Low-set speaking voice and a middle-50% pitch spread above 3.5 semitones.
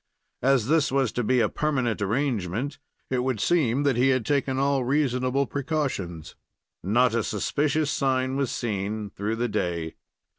Yes: low, 130 Hz; average, 4.1 semitones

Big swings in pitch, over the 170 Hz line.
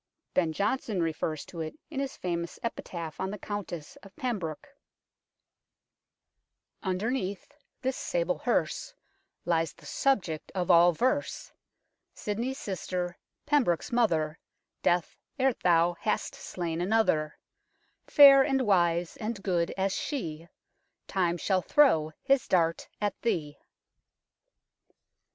Yes: wide, 6.0 semitones; medium, 185 Hz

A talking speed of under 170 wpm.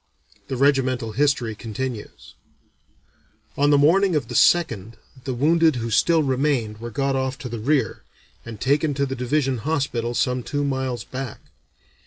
Yes: average, 155 wpm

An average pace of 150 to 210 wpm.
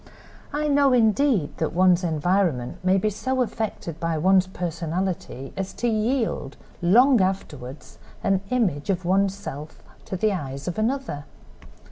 No: average, 140 wpm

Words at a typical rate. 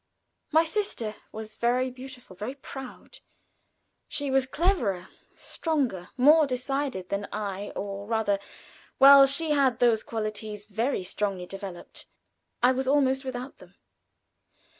No: slow, 120 wpm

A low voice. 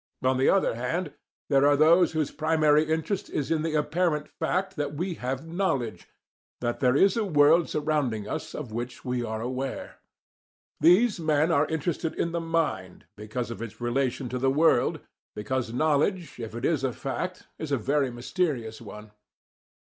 No: medium, 145 Hz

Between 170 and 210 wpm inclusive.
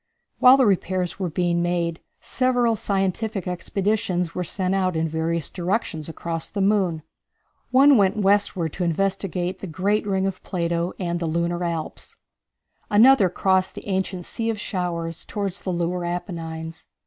No: average, 155 wpm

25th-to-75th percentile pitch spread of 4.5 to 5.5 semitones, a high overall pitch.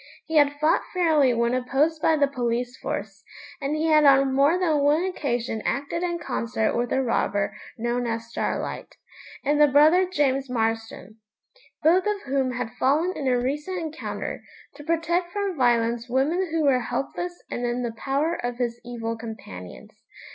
Yes: average, 4.9 semitones; very high, 275 Hz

